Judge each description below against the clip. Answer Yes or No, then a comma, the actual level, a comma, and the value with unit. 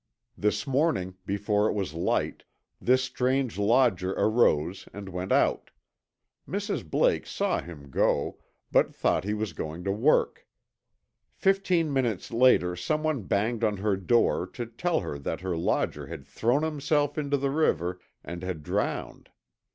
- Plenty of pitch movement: Yes, wide, 6.7 semitones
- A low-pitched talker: Yes, low, 105 Hz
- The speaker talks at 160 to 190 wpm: No, average, 145 wpm